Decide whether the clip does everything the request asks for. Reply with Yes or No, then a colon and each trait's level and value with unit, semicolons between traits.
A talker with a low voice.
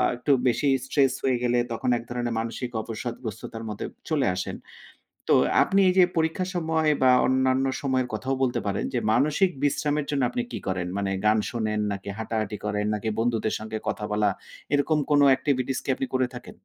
Yes: low, 125 Hz